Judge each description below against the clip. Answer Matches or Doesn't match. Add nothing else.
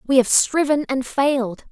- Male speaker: Doesn't match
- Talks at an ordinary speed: Matches